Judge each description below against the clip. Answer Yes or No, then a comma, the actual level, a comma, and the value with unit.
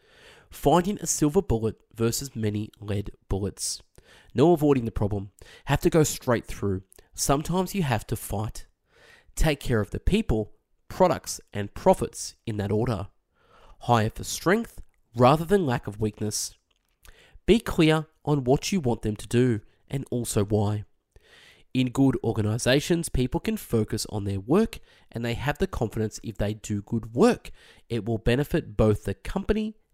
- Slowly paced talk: No, average, 155 wpm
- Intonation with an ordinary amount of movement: No, wide, 6.1 semitones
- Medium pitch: No, low, 115 Hz